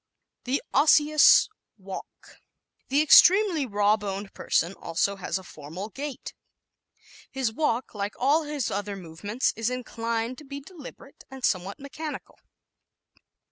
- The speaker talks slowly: Yes, slow, 130 wpm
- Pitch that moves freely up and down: Yes, wide, 6.0 semitones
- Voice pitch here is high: Yes, high, 235 Hz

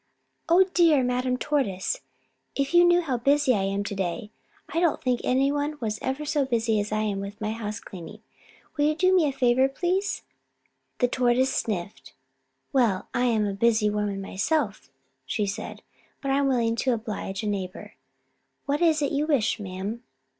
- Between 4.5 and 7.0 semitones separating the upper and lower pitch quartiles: Yes, wide, 5.4 semitones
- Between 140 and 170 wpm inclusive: No, average, 180 wpm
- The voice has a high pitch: Yes, high, 240 Hz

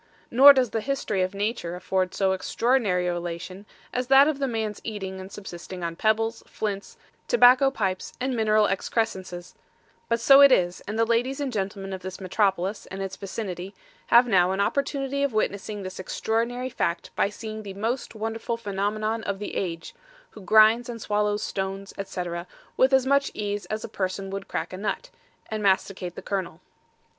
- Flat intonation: No, average, 3.6 semitones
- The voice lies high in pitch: Yes, high, 210 Hz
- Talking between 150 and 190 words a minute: Yes, average, 180 wpm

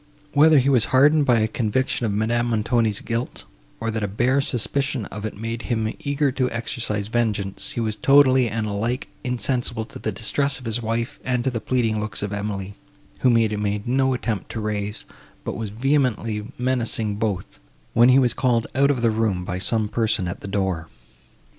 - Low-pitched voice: Yes, low, 115 Hz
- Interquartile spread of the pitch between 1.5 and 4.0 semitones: Yes, average, 3.1 semitones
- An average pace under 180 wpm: No, average, 190 wpm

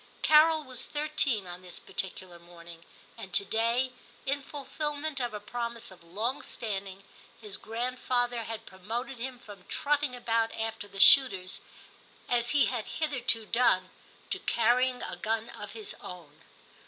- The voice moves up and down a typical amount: Yes, average, 4.8 semitones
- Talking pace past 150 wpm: No, average, 145 wpm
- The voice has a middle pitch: No, high, 230 Hz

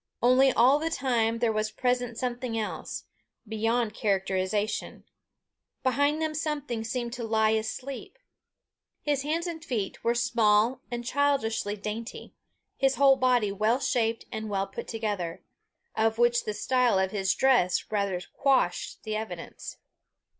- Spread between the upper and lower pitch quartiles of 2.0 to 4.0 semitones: Yes, average, 3.3 semitones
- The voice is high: Yes, high, 230 Hz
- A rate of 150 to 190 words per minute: No, average, 140 wpm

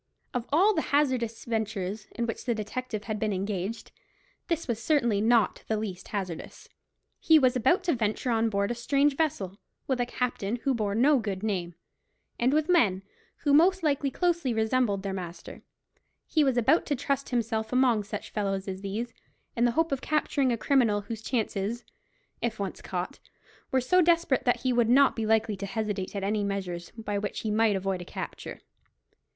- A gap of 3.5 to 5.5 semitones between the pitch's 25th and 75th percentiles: Yes, average, 4.5 semitones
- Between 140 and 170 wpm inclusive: No, average, 185 wpm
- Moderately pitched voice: No, high, 225 Hz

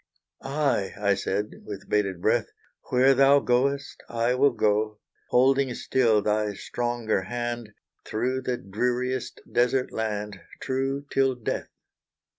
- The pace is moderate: No, slow, 120 wpm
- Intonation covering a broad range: No, average, 3.8 semitones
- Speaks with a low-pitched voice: Yes, low, 120 Hz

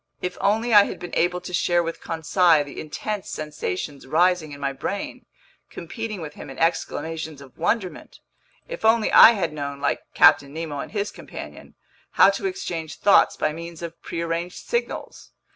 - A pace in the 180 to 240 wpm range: No, average, 170 wpm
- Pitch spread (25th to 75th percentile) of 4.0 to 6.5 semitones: Yes, average, 4.4 semitones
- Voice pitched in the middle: Yes, medium, 170 Hz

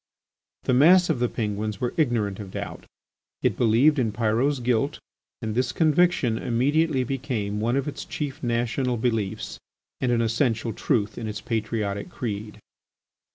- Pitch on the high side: No, low, 120 Hz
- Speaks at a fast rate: No, average, 150 wpm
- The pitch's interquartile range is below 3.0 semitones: No, average, 3.8 semitones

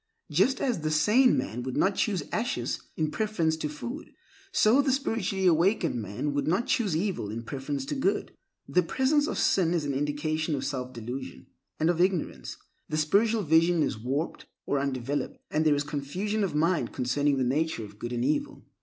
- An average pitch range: No, wide, 6.2 semitones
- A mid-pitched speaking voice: Yes, medium, 155 Hz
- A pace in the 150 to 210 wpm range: Yes, average, 190 wpm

